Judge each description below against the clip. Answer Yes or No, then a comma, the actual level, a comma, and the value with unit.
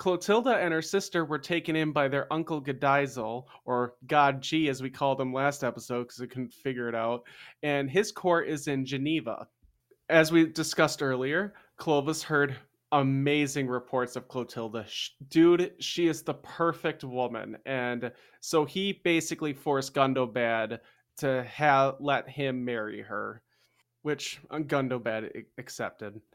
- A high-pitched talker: No, medium, 140 Hz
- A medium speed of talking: Yes, average, 145 wpm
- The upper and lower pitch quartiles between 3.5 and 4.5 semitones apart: Yes, average, 3.9 semitones